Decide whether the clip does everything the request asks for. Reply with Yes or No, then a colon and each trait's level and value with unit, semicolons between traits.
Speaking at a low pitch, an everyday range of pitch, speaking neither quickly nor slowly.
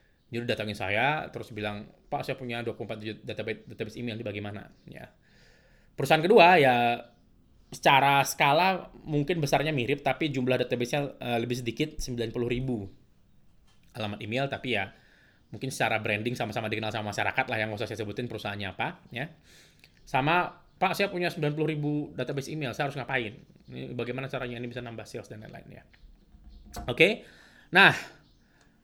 No: low, 120 Hz; average, 4.2 semitones; fast, 160 wpm